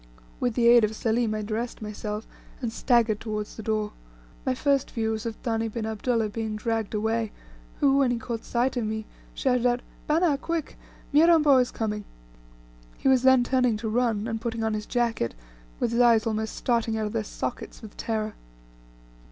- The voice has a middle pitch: No, high, 230 Hz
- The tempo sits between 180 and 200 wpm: Yes, average, 185 wpm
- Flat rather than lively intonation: Yes, narrow, 2.1 semitones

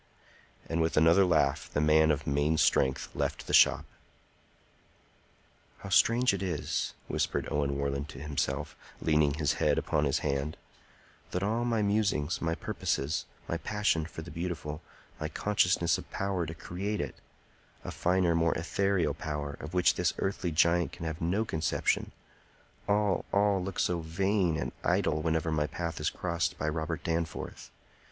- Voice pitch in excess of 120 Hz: No, very low, 80 Hz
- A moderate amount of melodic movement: Yes, average, 3.5 semitones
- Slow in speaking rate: No, average, 155 wpm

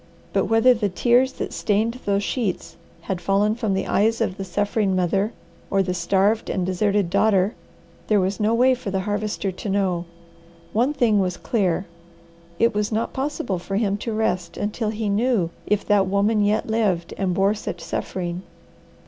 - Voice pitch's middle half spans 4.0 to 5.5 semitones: No, narrow, 2.6 semitones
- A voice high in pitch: Yes, high, 205 Hz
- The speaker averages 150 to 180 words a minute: Yes, average, 175 wpm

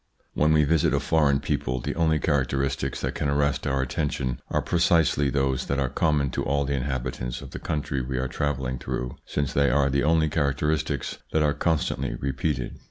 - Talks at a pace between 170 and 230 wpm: Yes, average, 195 wpm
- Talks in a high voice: No, very low, 70 Hz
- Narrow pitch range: Yes, narrow, 2.1 semitones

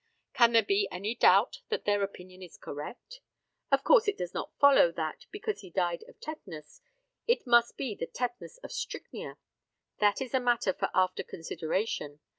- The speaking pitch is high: Yes, high, 205 Hz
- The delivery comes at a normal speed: Yes, average, 175 wpm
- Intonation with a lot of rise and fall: Yes, wide, 6.3 semitones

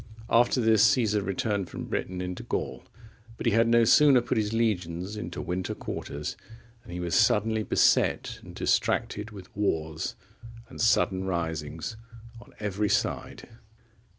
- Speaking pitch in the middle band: No, low, 100 Hz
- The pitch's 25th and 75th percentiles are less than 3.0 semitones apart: No, average, 4.2 semitones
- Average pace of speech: Yes, average, 145 wpm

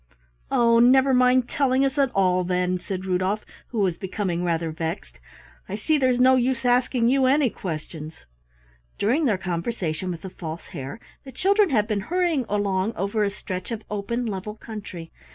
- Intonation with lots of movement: Yes, wide, 5.7 semitones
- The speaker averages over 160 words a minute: Yes, average, 170 wpm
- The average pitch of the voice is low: No, high, 210 Hz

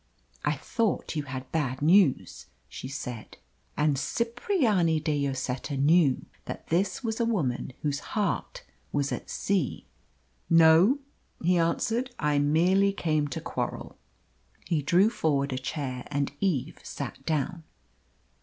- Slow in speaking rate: Yes, slow, 130 wpm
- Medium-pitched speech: Yes, medium, 155 Hz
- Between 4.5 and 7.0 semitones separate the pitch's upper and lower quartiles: Yes, wide, 5.5 semitones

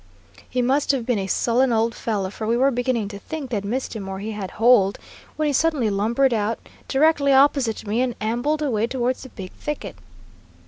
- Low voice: No, high, 240 Hz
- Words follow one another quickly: Yes, fast, 210 wpm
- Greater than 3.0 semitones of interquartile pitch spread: Yes, average, 4.0 semitones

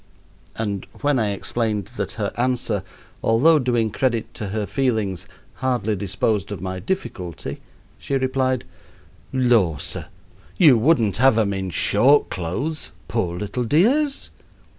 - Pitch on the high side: No, low, 115 Hz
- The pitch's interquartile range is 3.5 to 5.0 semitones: Yes, average, 4.6 semitones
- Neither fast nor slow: No, slow, 130 wpm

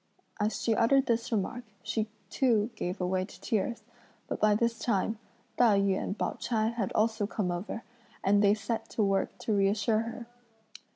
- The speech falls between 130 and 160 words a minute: No, average, 175 wpm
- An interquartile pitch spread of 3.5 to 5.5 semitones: No, narrow, 2.5 semitones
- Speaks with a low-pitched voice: No, high, 215 Hz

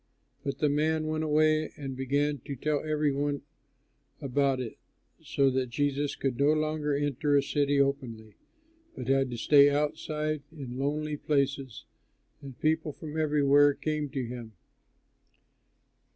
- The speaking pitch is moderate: Yes, medium, 145 Hz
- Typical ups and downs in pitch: No, narrow, 2.0 semitones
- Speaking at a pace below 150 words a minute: Yes, average, 140 wpm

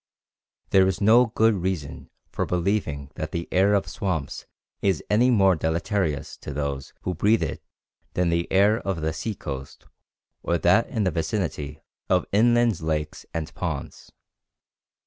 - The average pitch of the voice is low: Yes, very low, 90 Hz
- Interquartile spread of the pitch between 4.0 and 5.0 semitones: Yes, average, 4.7 semitones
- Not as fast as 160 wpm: Yes, average, 150 wpm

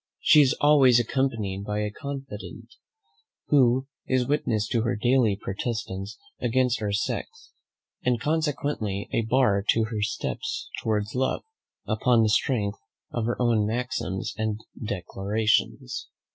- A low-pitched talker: Yes, low, 115 Hz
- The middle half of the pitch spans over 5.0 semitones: No, average, 3.7 semitones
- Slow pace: Yes, slow, 130 wpm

